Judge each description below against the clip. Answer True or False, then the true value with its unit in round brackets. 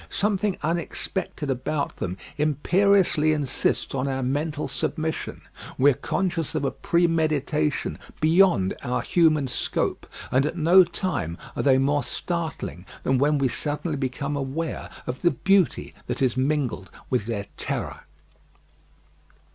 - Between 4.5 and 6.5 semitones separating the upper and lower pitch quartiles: False (4.1 semitones)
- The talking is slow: True (130 wpm)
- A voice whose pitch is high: False (150 Hz)